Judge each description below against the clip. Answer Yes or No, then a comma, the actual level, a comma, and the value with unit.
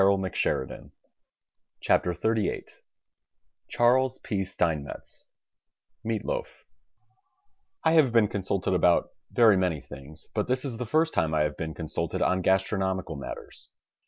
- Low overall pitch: Yes, very low, 95 Hz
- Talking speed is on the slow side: Yes, slow, 130 wpm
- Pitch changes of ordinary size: No, wide, 5.8 semitones